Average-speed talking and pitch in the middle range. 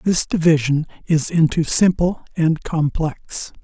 No: slow, 115 wpm; medium, 160 Hz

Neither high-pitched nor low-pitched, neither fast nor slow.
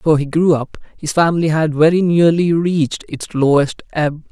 Yes: medium, 160 Hz; average, 180 wpm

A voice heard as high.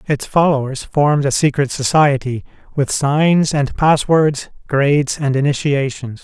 No: medium, 140 Hz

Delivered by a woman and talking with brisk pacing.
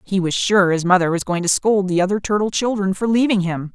Yes: female; fast, 255 wpm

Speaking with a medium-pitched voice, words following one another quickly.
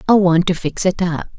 Yes: medium, 175 Hz; fast, 260 wpm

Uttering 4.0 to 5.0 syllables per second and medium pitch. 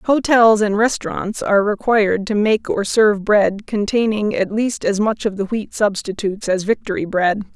No: 4.9 syllables/s; high, 210 Hz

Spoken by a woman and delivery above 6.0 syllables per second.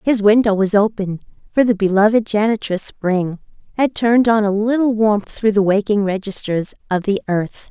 No: female; 5.0 syllables/s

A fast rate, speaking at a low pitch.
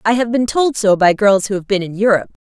No: fast, 295 wpm; high, 210 Hz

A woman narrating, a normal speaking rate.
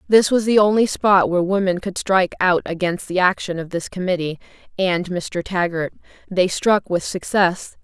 Yes: female; average, 175 wpm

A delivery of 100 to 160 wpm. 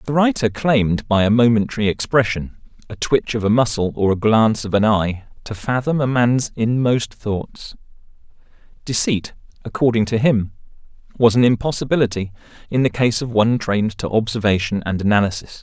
Yes: average, 155 wpm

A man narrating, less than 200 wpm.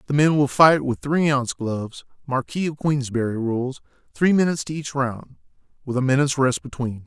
Yes: male; average, 180 wpm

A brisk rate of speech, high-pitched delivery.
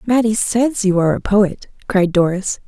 No: average, 180 wpm; high, 205 Hz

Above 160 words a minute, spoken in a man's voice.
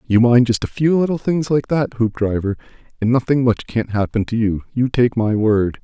Yes: fast, 205 wpm; male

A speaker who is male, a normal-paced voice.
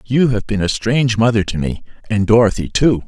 Yes: male; average, 195 wpm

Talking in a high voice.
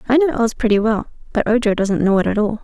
Yes: high, 225 Hz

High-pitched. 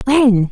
Yes: high, 235 Hz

